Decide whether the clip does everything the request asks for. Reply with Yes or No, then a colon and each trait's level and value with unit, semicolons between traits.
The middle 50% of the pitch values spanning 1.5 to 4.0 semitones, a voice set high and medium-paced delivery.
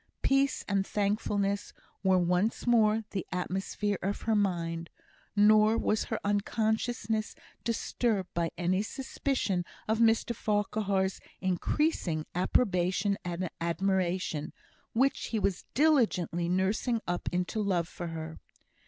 No: average, 3.5 semitones; high, 200 Hz; slow, 115 wpm